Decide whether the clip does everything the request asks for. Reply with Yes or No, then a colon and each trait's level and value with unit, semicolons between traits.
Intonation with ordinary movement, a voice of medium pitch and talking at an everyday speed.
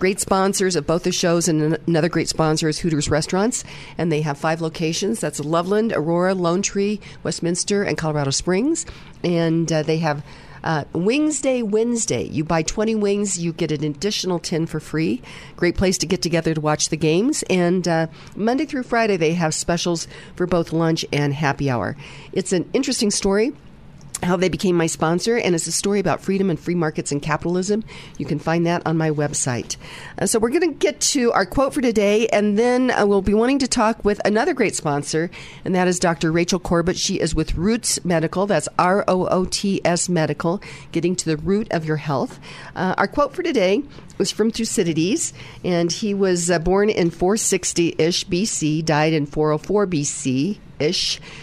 Yes: average, 4.1 semitones; medium, 170 Hz; average, 195 wpm